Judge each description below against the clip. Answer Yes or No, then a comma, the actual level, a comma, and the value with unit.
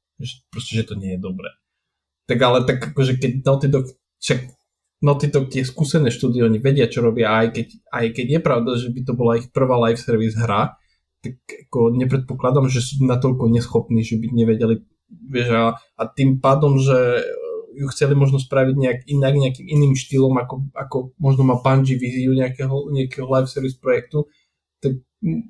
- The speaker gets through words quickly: Yes, fast, 175 wpm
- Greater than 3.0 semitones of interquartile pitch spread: No, narrow, 2.6 semitones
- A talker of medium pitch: No, low, 130 Hz